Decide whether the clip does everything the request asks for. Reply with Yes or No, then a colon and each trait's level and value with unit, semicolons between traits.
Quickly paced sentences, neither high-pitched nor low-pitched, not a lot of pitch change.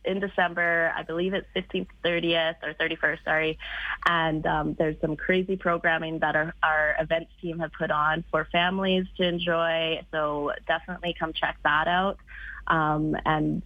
No: average, 160 wpm; medium, 165 Hz; narrow, 1.8 semitones